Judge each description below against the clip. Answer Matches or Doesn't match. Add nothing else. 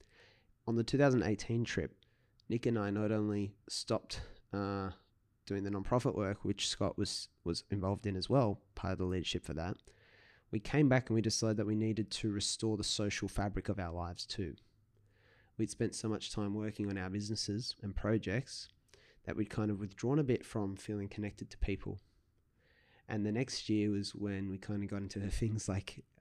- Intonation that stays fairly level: Matches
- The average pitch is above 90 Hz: Matches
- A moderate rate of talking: Matches